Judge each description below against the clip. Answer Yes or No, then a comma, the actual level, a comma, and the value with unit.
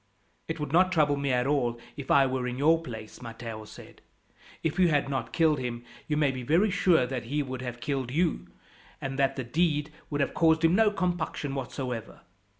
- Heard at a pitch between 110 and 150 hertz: Yes, medium, 140 Hz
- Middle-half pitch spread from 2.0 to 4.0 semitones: No, average, 4.4 semitones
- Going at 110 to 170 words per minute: No, fast, 205 wpm